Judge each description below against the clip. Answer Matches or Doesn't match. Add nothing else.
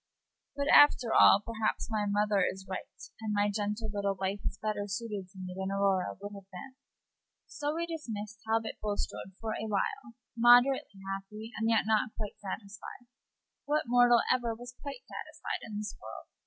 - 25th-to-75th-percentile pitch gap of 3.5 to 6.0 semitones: Doesn't match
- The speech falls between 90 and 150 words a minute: Doesn't match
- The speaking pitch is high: Matches